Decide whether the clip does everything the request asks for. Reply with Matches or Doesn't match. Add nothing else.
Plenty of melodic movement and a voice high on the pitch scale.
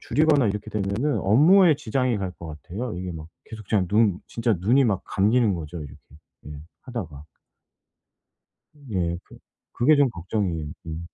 Doesn't match